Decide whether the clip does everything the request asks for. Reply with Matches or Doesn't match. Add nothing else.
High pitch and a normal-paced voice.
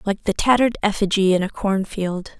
Matches